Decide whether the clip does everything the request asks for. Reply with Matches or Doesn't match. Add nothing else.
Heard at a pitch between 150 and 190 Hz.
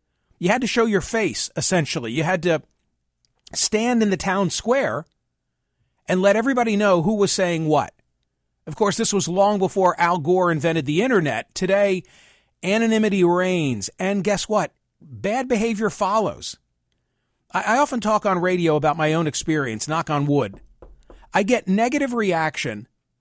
Matches